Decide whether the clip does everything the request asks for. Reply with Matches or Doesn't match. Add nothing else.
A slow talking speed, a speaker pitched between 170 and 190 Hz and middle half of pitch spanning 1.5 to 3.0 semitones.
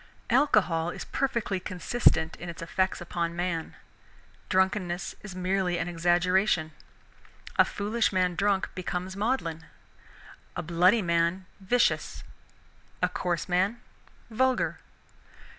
Matches